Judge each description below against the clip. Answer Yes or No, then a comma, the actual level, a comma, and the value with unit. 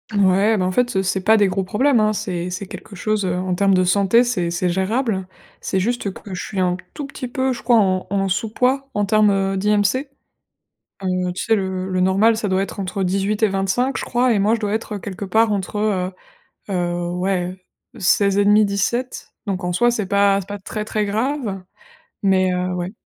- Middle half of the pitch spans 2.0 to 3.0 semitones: Yes, narrow, 2.6 semitones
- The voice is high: Yes, high, 200 Hz